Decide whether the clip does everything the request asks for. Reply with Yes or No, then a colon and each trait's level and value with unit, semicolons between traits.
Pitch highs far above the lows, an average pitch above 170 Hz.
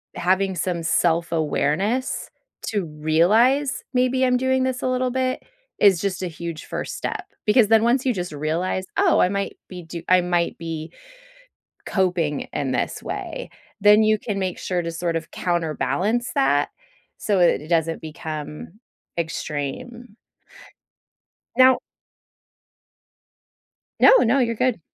Yes: wide, 6.3 semitones; medium, 185 Hz